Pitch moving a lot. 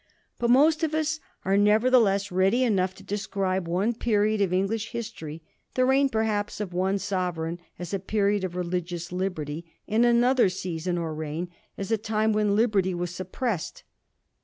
No: average, 3.7 semitones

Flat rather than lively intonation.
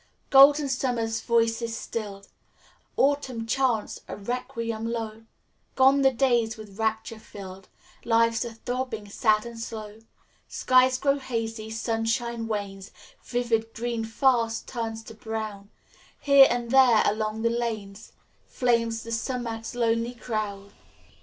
Yes: narrow, 1.8 semitones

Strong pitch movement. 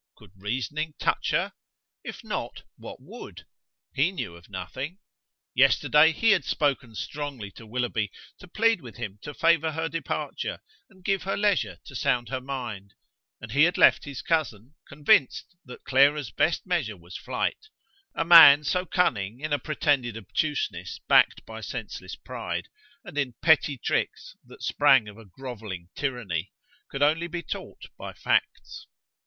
Yes: wide, 6.2 semitones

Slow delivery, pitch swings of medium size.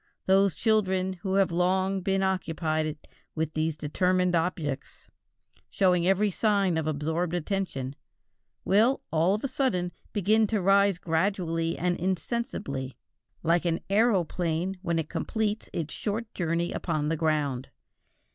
Yes: slow, 130 wpm; average, 3.4 semitones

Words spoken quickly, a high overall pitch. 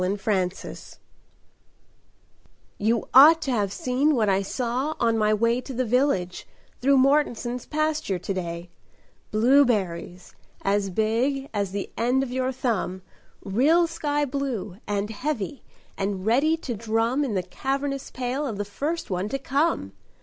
No: average, 140 wpm; high, 235 Hz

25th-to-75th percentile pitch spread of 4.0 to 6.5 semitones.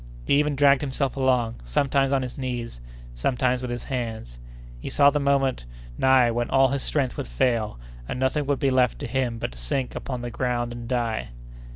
No: narrow, 2.4 semitones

